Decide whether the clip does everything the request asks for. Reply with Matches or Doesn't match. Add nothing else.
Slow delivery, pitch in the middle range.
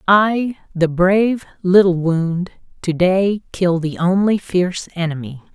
Matches